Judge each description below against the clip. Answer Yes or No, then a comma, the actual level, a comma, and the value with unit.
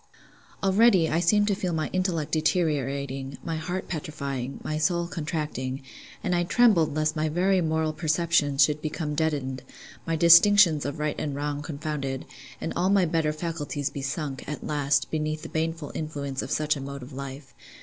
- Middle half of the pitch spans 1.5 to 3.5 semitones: Yes, average, 2.9 semitones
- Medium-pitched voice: Yes, medium, 155 Hz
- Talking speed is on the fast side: No, average, 170 wpm